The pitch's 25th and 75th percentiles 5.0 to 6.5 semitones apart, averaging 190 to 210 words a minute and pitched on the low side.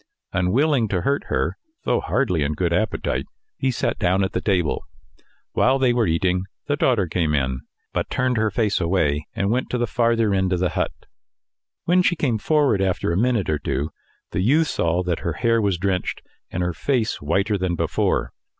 Yes: wide, 5.5 semitones; average, 195 wpm; very low, 95 Hz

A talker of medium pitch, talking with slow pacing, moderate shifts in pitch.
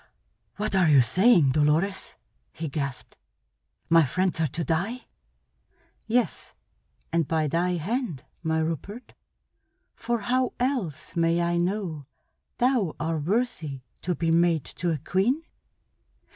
Yes: medium, 170 Hz; slow, 125 wpm; average, 4.8 semitones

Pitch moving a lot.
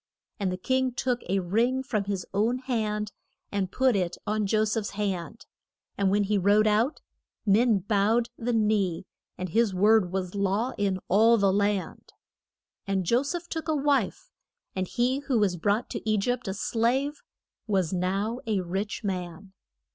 No: average, 3.5 semitones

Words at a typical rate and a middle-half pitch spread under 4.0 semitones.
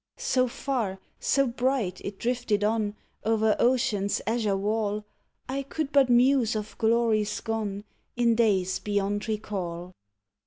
No: slow, 125 wpm; average, 3.0 semitones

